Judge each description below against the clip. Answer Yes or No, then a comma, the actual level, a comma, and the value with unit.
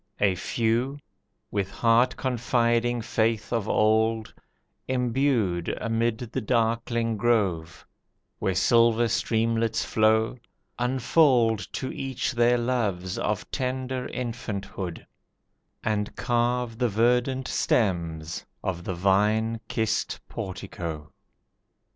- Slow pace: Yes, slow, 95 wpm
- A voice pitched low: Yes, low, 115 Hz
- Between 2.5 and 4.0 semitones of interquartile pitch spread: Yes, average, 2.9 semitones